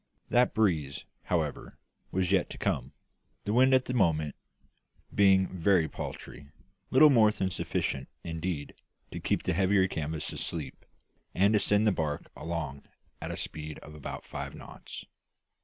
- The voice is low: Yes, very low, 90 Hz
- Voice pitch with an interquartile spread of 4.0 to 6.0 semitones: Yes, average, 4.9 semitones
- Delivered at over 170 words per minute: No, average, 150 wpm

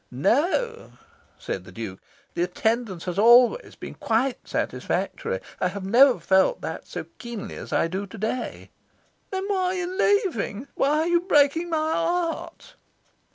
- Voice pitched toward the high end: Yes, very high, 275 Hz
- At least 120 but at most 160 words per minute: Yes, average, 155 wpm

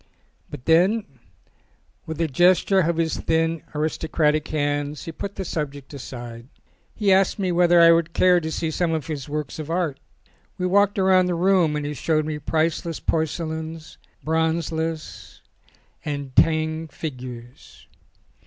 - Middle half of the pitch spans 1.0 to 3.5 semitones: Yes, narrow, 2.4 semitones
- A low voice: No, medium, 160 Hz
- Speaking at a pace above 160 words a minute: No, average, 150 wpm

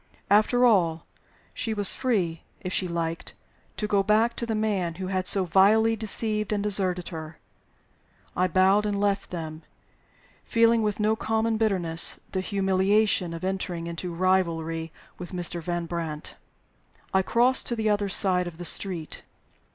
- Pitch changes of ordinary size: Yes, average, 3.7 semitones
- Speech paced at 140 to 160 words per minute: Yes, average, 155 wpm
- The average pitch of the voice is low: No, high, 190 Hz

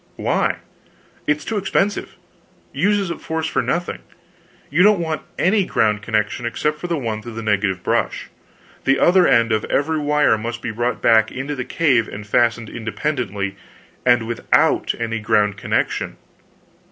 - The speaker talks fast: No, average, 155 wpm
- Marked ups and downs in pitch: Yes, wide, 6.2 semitones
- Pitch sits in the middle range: No, low, 120 Hz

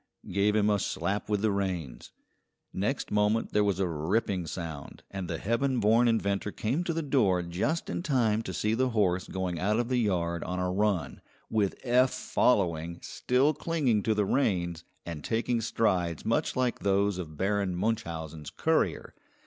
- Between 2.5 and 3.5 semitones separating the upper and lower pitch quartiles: No, average, 4.4 semitones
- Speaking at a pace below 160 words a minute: No, average, 175 wpm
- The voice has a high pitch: No, low, 100 Hz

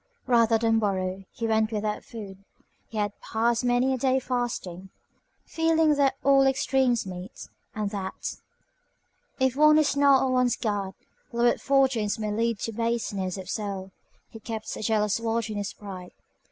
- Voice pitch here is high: Yes, high, 225 Hz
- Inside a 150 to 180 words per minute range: Yes, average, 160 wpm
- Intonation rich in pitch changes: No, average, 3.8 semitones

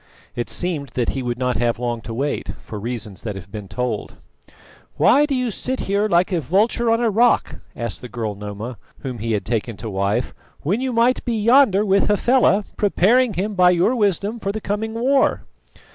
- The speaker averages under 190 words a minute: No, average, 200 wpm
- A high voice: No, medium, 180 Hz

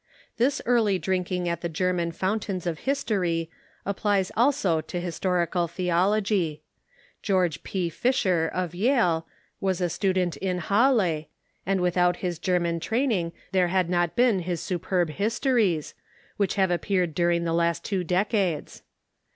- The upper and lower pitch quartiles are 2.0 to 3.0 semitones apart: Yes, average, 2.7 semitones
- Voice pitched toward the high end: No, medium, 180 Hz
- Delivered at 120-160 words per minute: Yes, average, 145 wpm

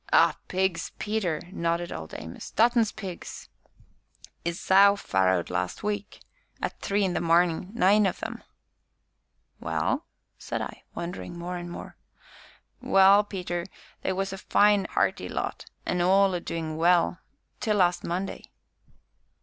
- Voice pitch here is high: No, medium, 180 Hz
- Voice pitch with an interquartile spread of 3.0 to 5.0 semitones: No, narrow, 2.6 semitones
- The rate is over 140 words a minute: No, slow, 135 wpm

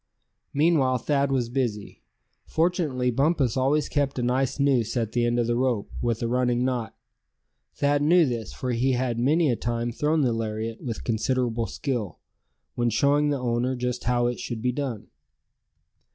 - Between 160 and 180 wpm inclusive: Yes, average, 170 wpm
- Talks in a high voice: No, low, 125 Hz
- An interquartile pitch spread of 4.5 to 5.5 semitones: No, average, 2.8 semitones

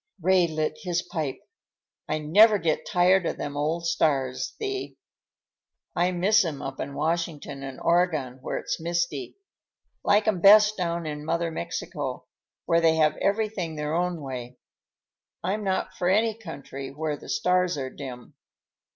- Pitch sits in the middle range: Yes, medium, 170 Hz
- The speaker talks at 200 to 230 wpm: No, average, 150 wpm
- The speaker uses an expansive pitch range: No, average, 3.7 semitones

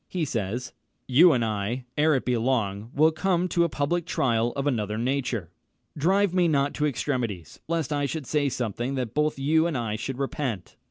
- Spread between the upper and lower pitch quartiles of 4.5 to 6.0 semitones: Yes, average, 4.8 semitones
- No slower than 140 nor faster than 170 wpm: No, average, 195 wpm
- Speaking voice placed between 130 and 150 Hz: Yes, low, 135 Hz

